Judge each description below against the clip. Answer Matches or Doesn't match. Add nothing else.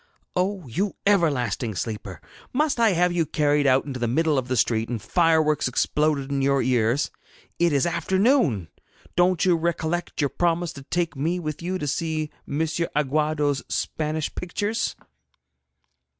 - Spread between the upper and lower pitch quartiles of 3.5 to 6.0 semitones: Matches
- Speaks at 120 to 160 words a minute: Matches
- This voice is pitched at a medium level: Matches